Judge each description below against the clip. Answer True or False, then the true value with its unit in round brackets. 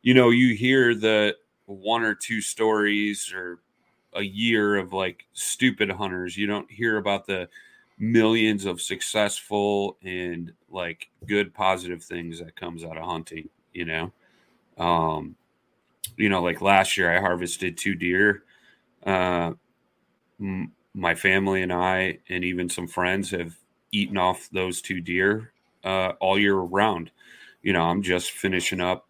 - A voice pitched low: True (95 Hz)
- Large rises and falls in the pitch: False (2.7 semitones)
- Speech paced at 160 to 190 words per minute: False (150 wpm)